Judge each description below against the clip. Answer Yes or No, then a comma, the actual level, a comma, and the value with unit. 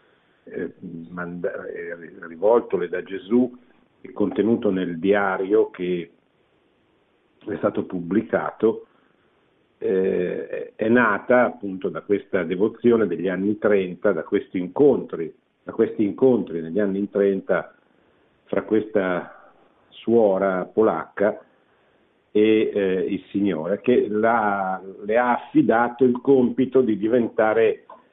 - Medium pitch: No, low, 105 Hz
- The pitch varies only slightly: No, average, 4.6 semitones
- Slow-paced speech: Yes, slow, 100 wpm